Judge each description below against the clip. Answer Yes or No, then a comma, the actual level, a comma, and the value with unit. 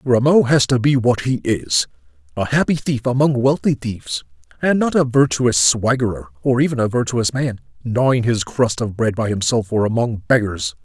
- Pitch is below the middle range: Yes, low, 115 Hz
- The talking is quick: No, average, 175 wpm